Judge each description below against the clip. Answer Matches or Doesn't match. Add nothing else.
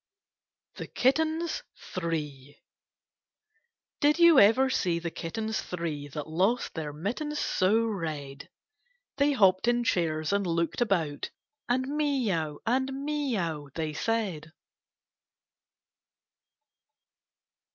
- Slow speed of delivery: Matches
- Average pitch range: Doesn't match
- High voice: Matches